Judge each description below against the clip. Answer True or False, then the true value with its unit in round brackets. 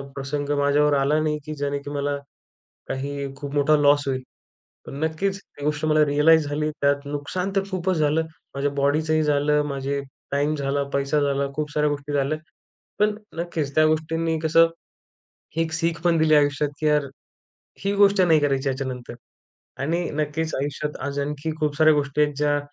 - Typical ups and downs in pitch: False (1.8 semitones)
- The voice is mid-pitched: True (150 Hz)